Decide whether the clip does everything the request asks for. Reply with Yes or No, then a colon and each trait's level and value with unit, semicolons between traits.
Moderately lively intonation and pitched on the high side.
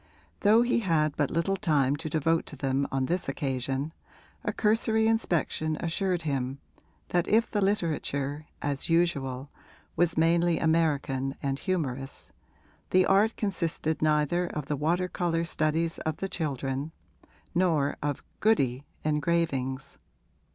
No: average, 3.9 semitones; medium, 160 Hz